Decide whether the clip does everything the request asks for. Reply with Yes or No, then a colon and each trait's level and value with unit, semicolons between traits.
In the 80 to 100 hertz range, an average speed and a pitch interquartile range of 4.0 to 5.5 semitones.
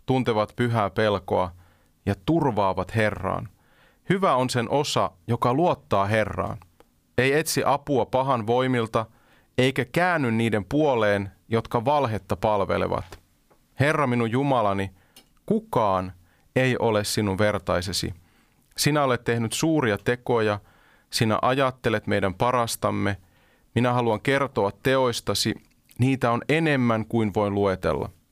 No: low, 115 Hz; average, 110 wpm; average, 4.3 semitones